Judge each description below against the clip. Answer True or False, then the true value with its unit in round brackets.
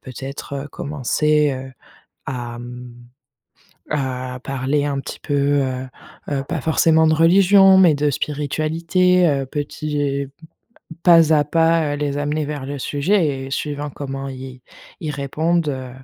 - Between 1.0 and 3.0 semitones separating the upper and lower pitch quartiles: True (2.7 semitones)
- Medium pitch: True (145 Hz)